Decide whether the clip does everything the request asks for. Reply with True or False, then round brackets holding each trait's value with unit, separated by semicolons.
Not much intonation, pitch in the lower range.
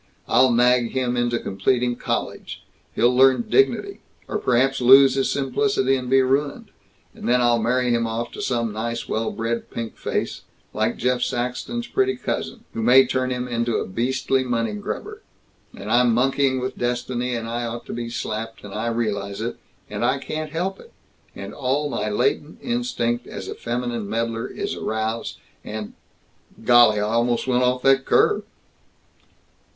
True (2.3 semitones; 120 Hz)